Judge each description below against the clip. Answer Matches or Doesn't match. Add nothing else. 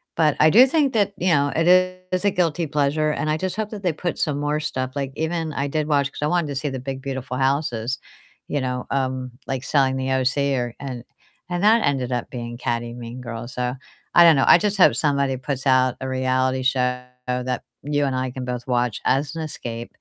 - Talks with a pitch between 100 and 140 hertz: Matches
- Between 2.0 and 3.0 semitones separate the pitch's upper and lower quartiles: Doesn't match